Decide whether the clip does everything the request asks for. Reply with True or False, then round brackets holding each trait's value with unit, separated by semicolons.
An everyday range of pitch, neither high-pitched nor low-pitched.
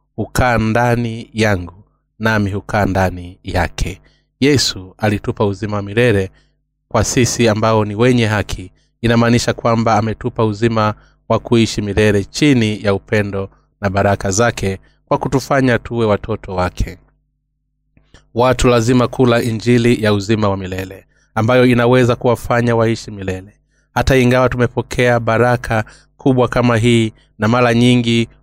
False (3.3 semitones; 115 Hz)